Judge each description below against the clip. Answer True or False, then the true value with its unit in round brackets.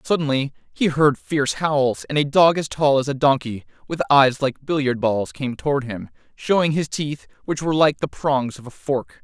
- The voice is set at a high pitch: False (140 Hz)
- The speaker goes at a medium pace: False (210 wpm)